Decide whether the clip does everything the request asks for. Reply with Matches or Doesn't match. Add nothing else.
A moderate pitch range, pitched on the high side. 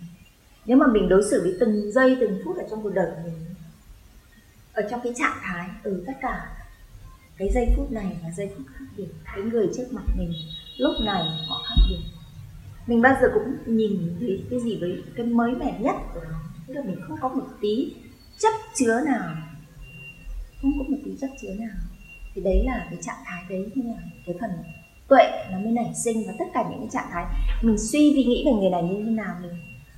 Doesn't match